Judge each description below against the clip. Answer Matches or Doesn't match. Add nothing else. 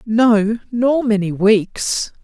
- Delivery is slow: Matches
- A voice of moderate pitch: Doesn't match